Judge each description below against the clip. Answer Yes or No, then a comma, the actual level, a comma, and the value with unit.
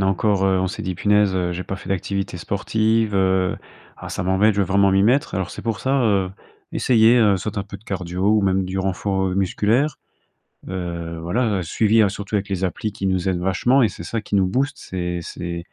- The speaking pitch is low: Yes, very low, 95 Hz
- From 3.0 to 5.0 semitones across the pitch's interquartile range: No, narrow, 2.4 semitones